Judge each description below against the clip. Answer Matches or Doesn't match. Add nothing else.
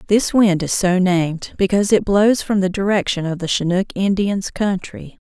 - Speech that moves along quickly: Doesn't match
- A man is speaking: Doesn't match